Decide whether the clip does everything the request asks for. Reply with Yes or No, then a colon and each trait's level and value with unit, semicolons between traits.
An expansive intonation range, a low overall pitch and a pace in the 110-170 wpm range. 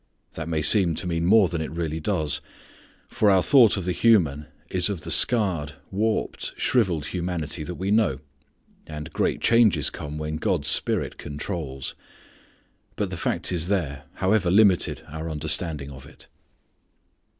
No: average, 4.1 semitones; very low, 85 Hz; average, 155 wpm